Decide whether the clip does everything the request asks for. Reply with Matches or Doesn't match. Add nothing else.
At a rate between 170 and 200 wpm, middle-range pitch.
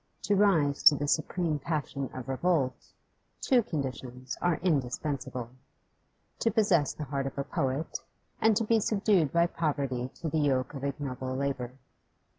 Doesn't match